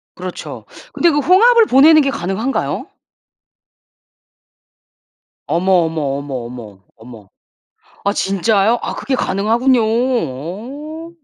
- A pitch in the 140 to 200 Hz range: No, high, 220 Hz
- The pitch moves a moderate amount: No, wide, 8.1 semitones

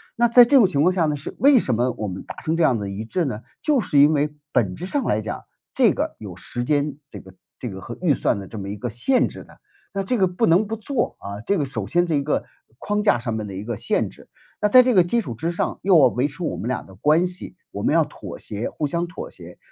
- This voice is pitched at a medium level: Yes, medium, 150 Hz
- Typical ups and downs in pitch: No, wide, 9.0 semitones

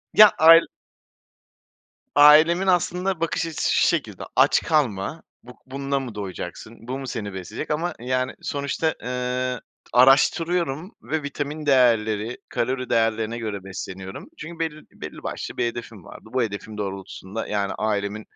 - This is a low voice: Yes, low, 125 Hz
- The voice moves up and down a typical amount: No, wide, 6.0 semitones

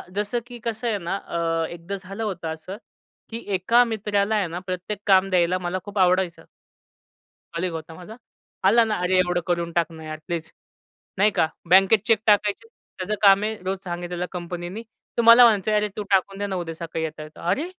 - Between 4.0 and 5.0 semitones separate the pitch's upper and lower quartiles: No, average, 3.4 semitones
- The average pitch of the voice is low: No, medium, 185 Hz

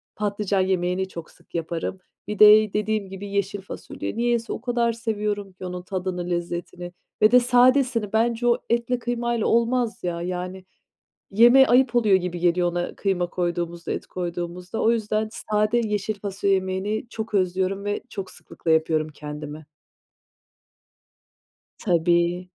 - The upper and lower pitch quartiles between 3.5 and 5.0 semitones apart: Yes, average, 3.9 semitones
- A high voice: Yes, high, 195 Hz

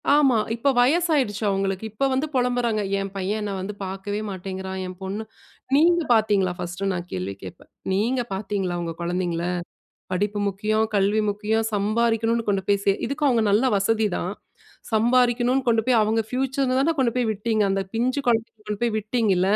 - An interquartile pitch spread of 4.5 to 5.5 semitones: No, average, 3.8 semitones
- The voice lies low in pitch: No, high, 215 Hz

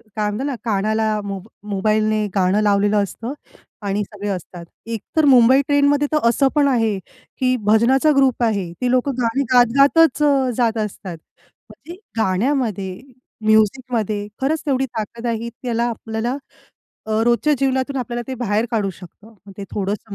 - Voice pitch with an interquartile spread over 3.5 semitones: Yes, average, 4.0 semitones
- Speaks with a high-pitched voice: Yes, high, 230 Hz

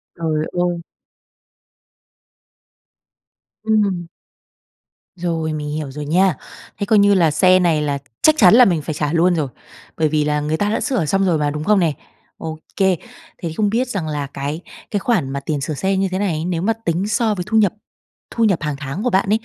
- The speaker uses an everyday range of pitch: Yes, average, 4.7 semitones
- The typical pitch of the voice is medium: Yes, medium, 170 Hz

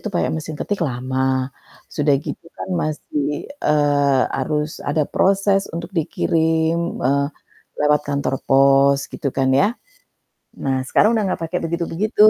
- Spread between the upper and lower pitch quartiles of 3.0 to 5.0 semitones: Yes, average, 3.3 semitones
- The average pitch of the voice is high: No, medium, 150 Hz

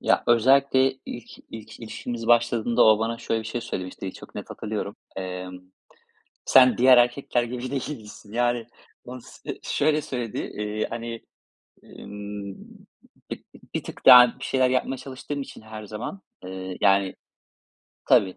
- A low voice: Yes, low, 115 Hz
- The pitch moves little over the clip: No, average, 3.1 semitones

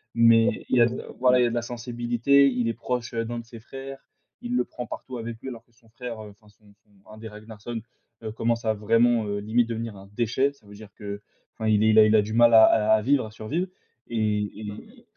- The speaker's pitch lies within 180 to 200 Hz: No, low, 115 Hz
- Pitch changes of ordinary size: No, narrow, 2.0 semitones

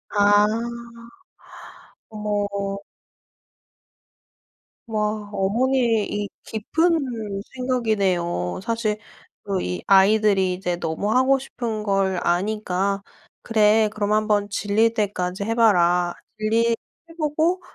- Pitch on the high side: Yes, high, 210 Hz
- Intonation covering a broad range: No, narrow, 2.6 semitones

